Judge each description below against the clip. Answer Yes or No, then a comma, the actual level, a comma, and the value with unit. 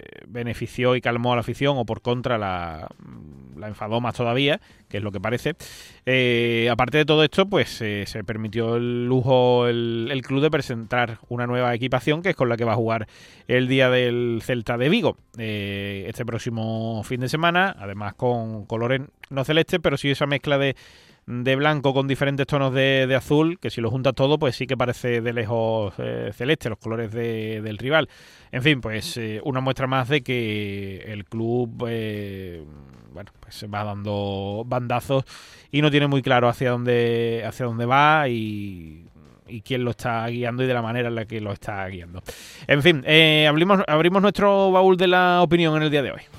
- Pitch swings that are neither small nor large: Yes, average, 3.5 semitones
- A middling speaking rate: No, fast, 200 wpm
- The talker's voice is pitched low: Yes, low, 120 Hz